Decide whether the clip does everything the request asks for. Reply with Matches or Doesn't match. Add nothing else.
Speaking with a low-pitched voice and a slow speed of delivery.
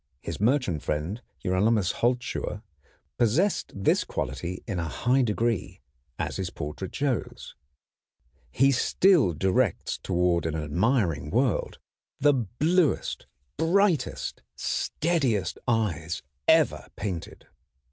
Matches